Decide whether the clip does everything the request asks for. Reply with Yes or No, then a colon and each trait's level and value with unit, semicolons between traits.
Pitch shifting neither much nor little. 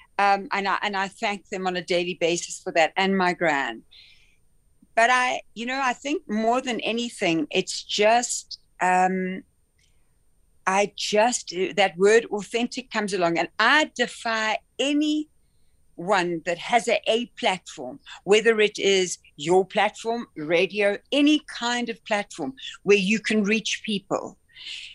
Yes: average, 4.0 semitones